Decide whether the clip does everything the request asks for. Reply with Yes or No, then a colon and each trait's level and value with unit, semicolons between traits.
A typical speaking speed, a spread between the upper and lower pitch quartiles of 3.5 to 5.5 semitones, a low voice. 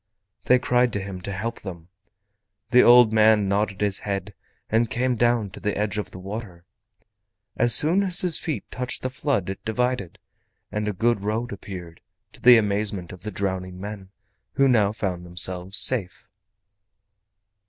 Yes: average, 165 wpm; average, 3.8 semitones; low, 105 Hz